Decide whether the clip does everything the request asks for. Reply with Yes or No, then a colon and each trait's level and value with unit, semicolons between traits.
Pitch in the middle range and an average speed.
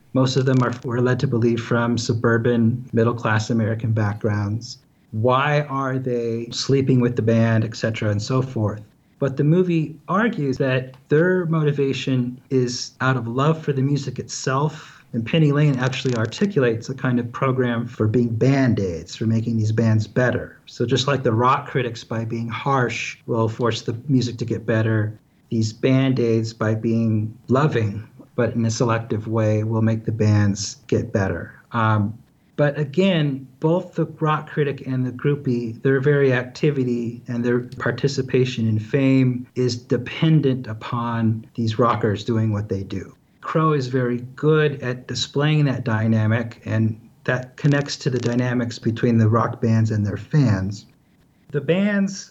No: low, 125 Hz; average, 160 wpm